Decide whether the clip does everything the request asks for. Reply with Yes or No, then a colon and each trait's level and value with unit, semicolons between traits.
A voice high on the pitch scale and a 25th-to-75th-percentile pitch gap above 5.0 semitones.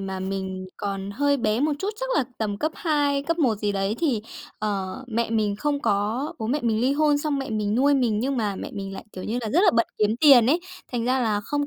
Yes: high, 230 Hz; wide, 5.6 semitones